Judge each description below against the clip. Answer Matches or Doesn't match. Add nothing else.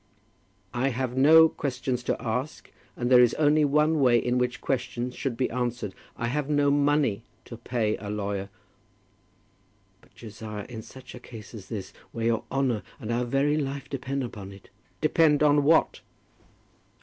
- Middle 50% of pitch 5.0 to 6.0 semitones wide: Doesn't match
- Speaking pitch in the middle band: Doesn't match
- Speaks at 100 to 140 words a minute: Doesn't match